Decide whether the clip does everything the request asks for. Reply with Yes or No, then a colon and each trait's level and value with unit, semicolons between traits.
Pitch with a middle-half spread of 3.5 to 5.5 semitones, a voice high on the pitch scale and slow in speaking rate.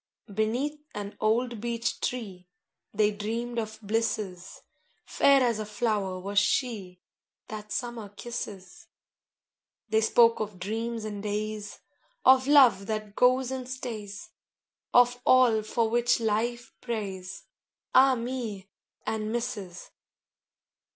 No: average, 2.8 semitones; high, 220 Hz; slow, 115 wpm